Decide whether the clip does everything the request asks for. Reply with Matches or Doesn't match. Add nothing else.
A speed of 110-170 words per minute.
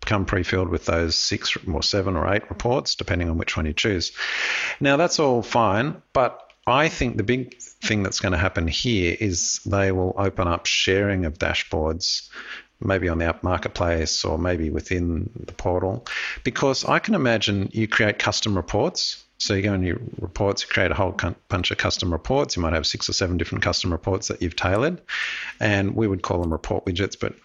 Doesn't match